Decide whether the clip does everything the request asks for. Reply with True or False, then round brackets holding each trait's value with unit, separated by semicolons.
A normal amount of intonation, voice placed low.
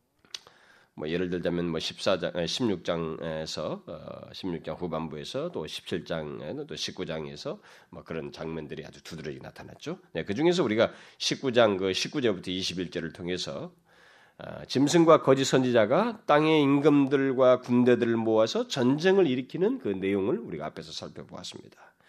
False (8.6 semitones; 115 Hz)